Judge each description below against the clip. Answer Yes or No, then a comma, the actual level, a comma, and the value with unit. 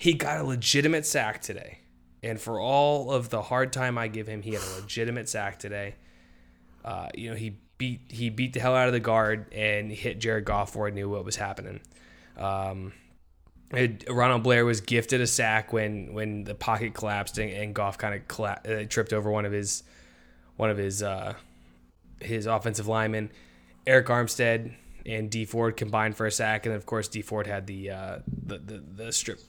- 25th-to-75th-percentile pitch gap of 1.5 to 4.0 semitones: Yes, narrow, 2.6 semitones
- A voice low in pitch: Yes, low, 110 Hz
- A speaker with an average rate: Yes, average, 195 wpm